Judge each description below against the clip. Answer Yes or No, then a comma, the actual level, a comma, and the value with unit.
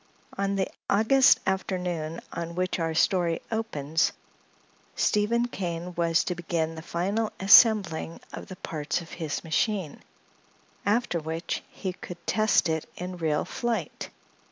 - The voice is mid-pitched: Yes, medium, 180 Hz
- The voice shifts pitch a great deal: No, average, 3.6 semitones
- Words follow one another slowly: Yes, slow, 130 wpm